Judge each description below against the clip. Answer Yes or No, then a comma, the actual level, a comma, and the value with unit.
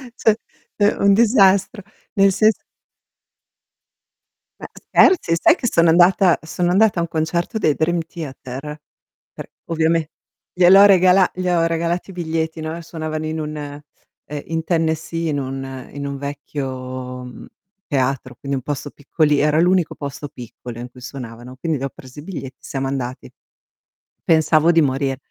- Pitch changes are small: No, average, 4.1 semitones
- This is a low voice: No, medium, 160 Hz